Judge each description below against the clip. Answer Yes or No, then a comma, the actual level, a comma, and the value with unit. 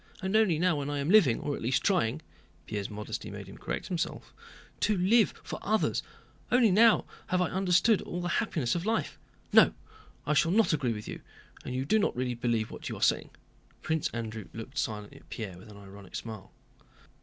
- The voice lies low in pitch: No, medium, 145 Hz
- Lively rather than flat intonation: Yes, wide, 8.8 semitones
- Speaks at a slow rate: No, average, 200 wpm